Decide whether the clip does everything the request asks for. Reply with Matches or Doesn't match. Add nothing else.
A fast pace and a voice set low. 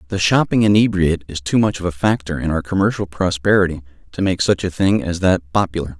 Matches